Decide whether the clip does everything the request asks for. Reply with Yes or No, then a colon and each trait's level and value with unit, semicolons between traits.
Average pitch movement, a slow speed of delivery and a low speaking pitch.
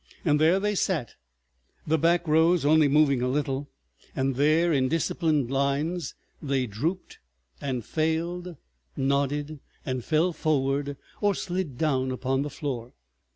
No: average, 3.3 semitones; slow, 130 wpm; medium, 150 Hz